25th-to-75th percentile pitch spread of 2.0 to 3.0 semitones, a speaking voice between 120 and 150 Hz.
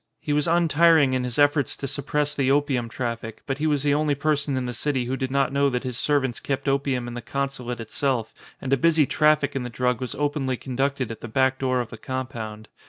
Yes: narrow, 2.6 semitones; low, 135 Hz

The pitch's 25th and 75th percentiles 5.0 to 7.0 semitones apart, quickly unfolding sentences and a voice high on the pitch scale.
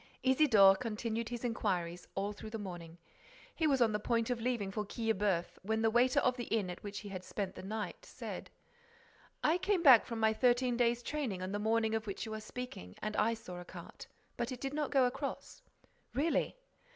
No: average, 3.5 semitones; fast, 210 wpm; high, 225 Hz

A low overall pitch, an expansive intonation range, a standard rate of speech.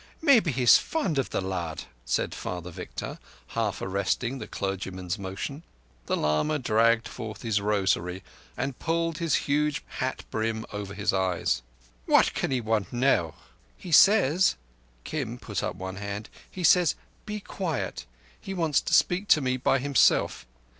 Yes: low, 115 Hz; wide, 7.9 semitones; average, 150 wpm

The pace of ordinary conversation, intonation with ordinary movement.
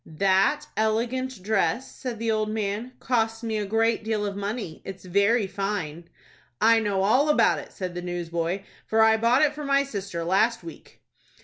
Yes: average, 180 wpm; average, 3.1 semitones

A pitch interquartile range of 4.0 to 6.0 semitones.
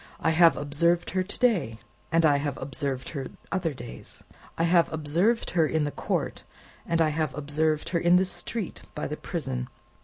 No: average, 3.0 semitones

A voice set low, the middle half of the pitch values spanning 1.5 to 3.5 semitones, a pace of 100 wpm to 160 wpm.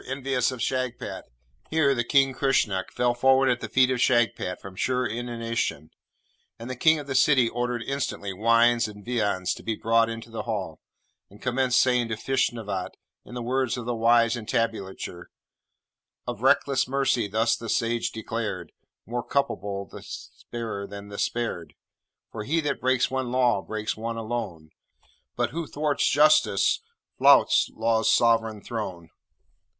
Yes: low, 115 Hz; average, 2.9 semitones; average, 155 wpm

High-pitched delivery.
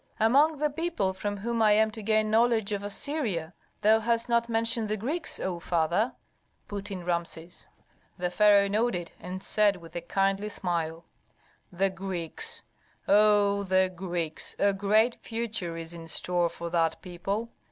Yes: high, 200 Hz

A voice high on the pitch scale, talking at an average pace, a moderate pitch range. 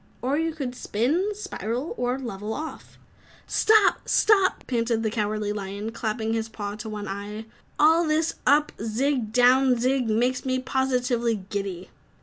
Yes: high, 240 Hz; average, 155 wpm; average, 4.0 semitones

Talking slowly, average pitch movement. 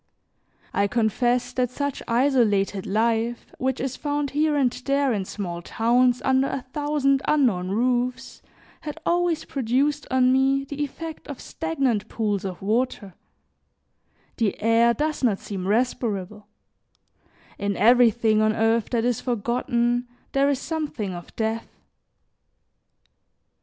Yes: slow, 125 wpm; average, 4.0 semitones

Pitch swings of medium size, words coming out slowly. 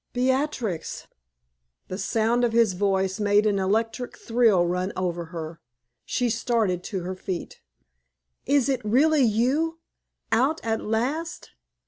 Yes: average, 4.8 semitones; slow, 125 wpm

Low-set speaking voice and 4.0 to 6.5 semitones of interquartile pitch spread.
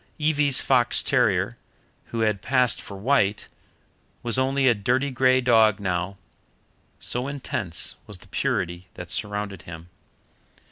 Yes: low, 115 Hz; average, 5.0 semitones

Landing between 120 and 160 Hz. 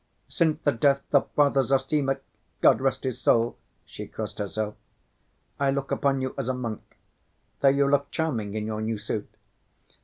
Yes: low, 135 Hz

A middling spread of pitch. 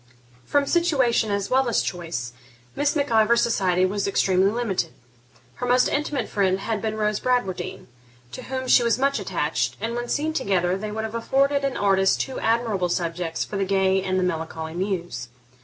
Yes: average, 4.8 semitones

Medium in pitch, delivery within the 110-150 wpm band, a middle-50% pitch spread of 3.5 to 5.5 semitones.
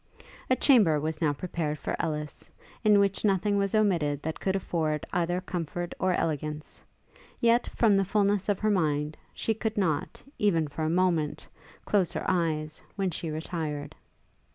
No: medium, 175 Hz; average, 160 wpm; average, 4.5 semitones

